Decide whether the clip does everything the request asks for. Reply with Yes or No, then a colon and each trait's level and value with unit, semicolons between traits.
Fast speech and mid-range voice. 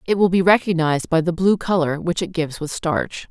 Yes: fast, 235 wpm; medium, 175 Hz